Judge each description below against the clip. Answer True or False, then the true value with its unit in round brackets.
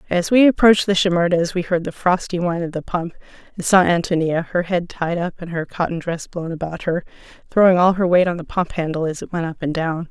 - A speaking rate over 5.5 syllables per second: True (5.9 syllables/s)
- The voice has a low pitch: False (175 Hz)